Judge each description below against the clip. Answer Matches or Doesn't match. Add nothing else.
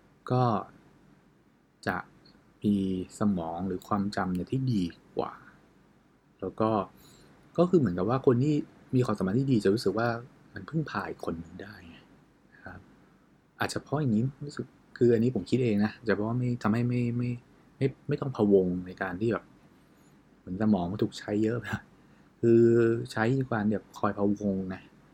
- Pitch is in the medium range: Doesn't match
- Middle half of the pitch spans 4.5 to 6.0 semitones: Doesn't match